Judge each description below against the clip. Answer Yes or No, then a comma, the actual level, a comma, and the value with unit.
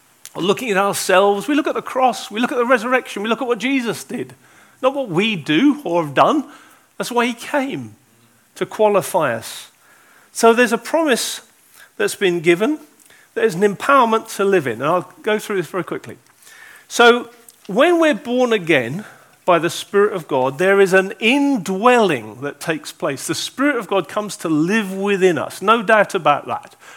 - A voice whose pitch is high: Yes, high, 215 Hz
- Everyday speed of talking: Yes, average, 185 wpm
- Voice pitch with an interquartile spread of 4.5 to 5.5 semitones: Yes, average, 5.2 semitones